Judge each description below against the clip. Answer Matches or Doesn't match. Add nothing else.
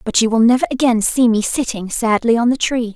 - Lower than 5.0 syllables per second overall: Doesn't match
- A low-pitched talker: Doesn't match